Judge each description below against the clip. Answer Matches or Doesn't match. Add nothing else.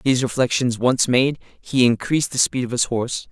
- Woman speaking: Doesn't match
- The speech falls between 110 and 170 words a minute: Doesn't match